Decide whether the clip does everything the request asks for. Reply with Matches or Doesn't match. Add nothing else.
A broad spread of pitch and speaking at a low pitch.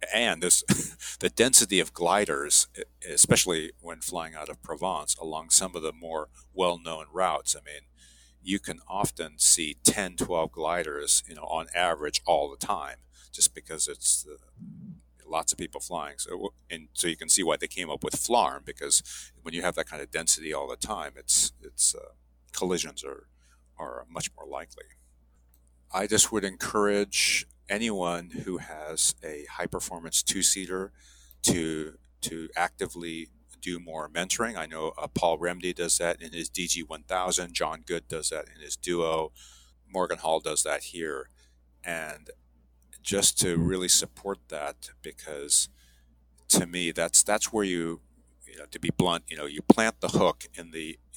Matches